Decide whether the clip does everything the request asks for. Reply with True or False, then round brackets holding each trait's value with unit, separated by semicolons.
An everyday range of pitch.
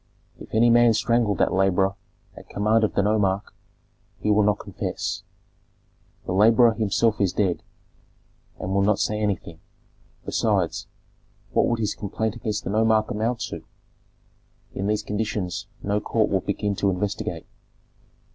False (1.9 semitones)